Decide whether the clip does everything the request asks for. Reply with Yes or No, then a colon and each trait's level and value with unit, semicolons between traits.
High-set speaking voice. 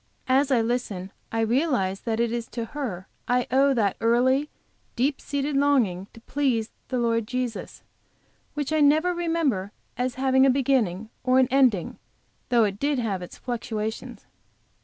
Yes: very high, 250 Hz